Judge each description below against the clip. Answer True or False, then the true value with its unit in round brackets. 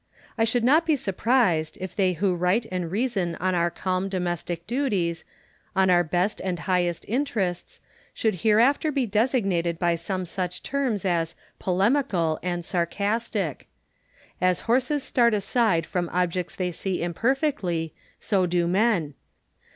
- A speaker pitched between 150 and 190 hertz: True (185 Hz)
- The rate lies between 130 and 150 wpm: True (140 wpm)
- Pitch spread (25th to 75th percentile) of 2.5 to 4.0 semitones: False (4.7 semitones)